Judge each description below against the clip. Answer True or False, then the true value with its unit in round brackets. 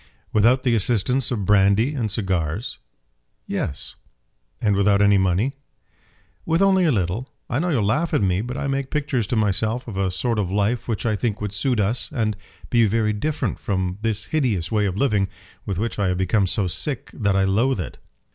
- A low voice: True (105 Hz)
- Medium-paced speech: True (195 wpm)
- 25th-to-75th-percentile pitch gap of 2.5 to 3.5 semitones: False (4.1 semitones)